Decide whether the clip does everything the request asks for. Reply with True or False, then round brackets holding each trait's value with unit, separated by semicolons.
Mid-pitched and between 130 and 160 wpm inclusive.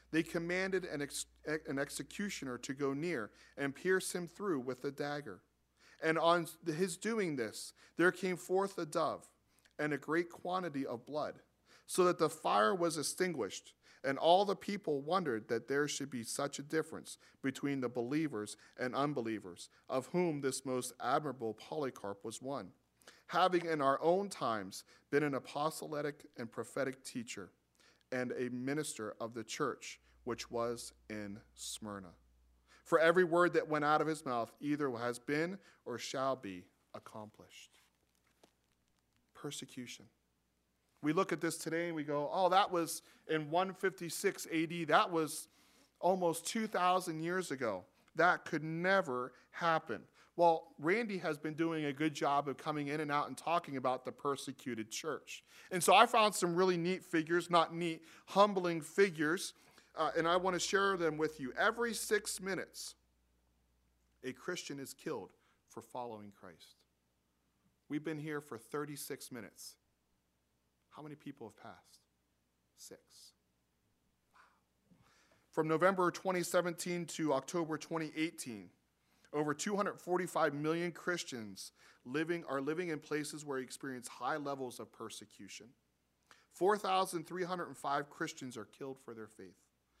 True (150 Hz; 145 wpm)